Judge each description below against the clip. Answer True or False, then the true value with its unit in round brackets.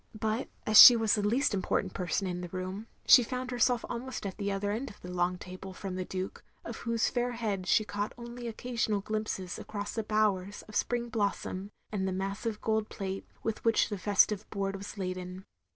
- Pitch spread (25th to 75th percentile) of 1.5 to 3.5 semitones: True (3.0 semitones)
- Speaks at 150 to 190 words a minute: False (200 wpm)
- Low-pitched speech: False (205 Hz)